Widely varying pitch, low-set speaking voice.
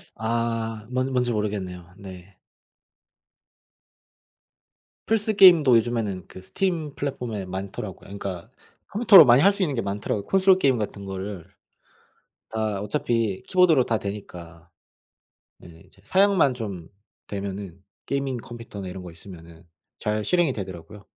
Yes: wide, 5.8 semitones; low, 105 Hz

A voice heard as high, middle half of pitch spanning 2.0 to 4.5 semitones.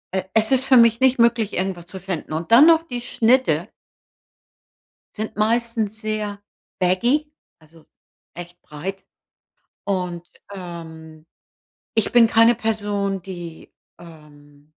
No: high, 200 Hz; average, 5.1 semitones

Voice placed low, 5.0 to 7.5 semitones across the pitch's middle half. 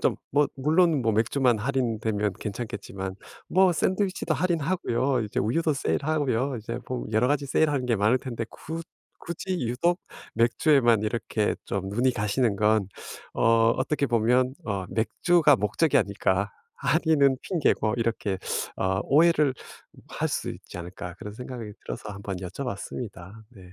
Yes: low, 120 Hz; wide, 5.4 semitones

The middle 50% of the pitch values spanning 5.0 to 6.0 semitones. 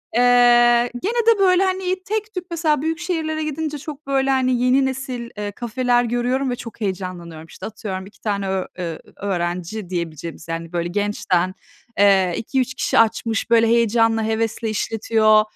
Yes: wide, 5.4 semitones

